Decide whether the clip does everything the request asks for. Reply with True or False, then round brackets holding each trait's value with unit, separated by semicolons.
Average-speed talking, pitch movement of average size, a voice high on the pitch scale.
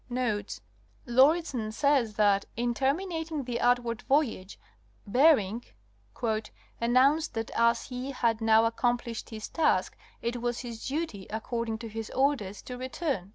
False (125 wpm; 3.3 semitones; 240 Hz)